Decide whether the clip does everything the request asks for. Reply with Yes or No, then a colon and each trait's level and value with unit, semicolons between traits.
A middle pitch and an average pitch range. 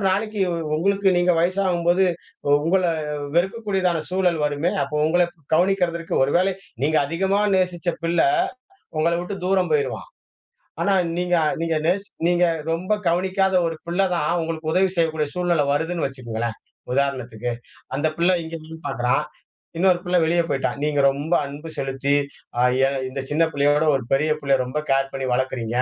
Yes: medium, 165 Hz; average, 4.1 semitones